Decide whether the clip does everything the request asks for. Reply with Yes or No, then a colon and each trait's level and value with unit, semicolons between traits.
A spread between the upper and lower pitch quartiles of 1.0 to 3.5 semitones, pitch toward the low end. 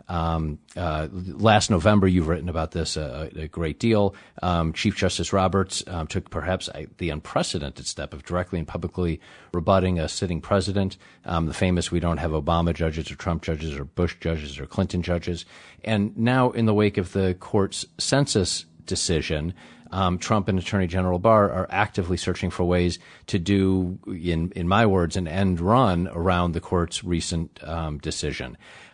Yes: average, 2.8 semitones; very low, 90 Hz